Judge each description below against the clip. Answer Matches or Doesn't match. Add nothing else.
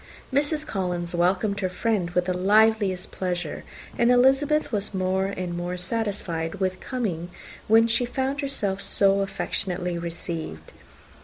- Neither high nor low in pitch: Doesn't match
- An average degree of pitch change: Matches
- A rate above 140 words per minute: Doesn't match